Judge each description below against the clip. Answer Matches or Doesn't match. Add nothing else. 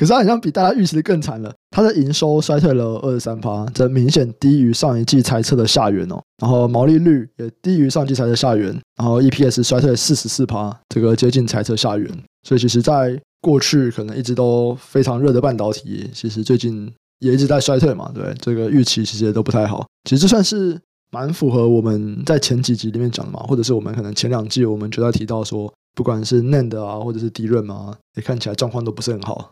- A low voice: Matches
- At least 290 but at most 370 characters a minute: Matches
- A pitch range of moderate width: Matches